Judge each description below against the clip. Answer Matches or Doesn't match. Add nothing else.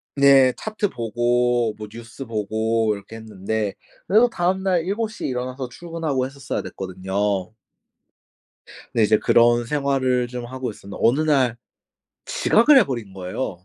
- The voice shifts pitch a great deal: Doesn't match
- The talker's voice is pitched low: Matches